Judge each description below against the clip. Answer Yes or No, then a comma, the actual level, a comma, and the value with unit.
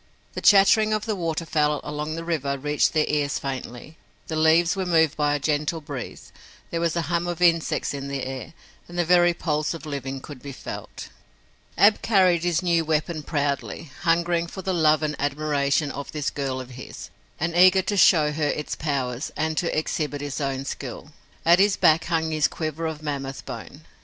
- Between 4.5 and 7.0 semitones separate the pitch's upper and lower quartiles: No, average, 2.9 semitones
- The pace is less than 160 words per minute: No, average, 190 wpm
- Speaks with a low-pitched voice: No, medium, 155 Hz